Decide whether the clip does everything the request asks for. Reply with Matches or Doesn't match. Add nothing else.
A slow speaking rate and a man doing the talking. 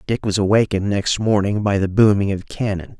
Doesn't match